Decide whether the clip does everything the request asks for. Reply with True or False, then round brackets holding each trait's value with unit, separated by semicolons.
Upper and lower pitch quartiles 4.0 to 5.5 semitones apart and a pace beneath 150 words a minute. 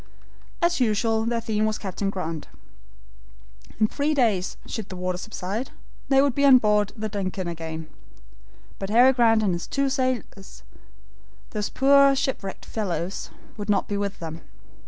False (4.7 semitones; 155 wpm)